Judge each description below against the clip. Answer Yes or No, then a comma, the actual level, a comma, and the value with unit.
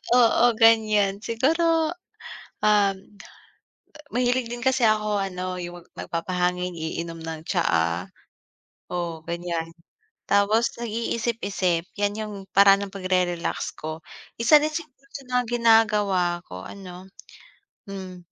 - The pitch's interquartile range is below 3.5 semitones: No, average, 4.3 semitones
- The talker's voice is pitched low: No, high, 195 Hz